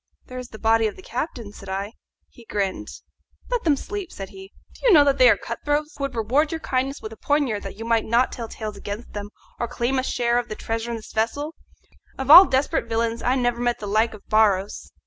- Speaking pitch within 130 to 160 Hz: No, high, 235 Hz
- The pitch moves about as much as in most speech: Yes, average, 4.2 semitones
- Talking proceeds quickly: Yes, fast, 240 wpm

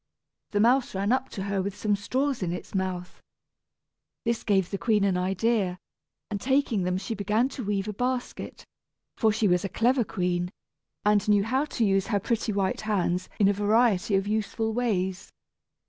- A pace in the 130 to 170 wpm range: No, average, 180 wpm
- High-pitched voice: Yes, high, 205 Hz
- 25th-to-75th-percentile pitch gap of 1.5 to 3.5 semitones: Yes, average, 3.1 semitones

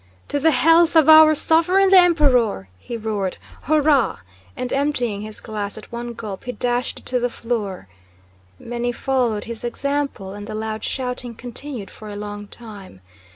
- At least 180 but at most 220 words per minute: No, average, 165 wpm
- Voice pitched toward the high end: Yes, high, 240 Hz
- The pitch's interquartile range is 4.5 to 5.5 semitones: Yes, average, 5.0 semitones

